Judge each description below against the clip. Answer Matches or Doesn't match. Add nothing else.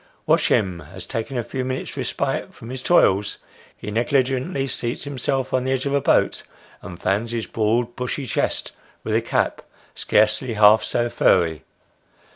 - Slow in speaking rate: Doesn't match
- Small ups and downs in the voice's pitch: Doesn't match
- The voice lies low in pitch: Matches